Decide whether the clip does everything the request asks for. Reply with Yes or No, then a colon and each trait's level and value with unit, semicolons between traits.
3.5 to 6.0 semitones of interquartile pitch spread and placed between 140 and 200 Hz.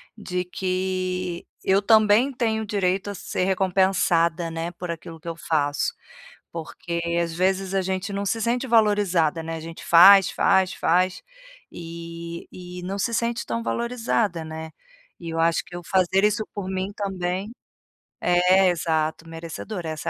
No: average, 2.9 semitones; medium, 185 Hz